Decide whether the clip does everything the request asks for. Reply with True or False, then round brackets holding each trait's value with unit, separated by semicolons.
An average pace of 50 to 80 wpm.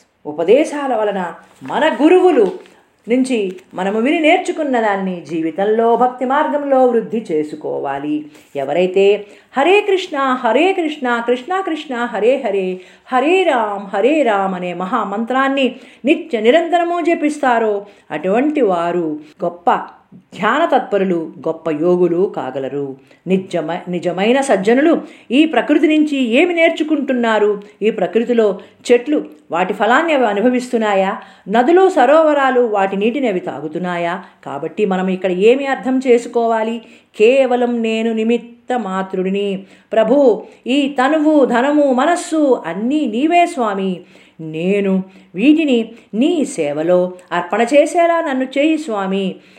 False (105 wpm)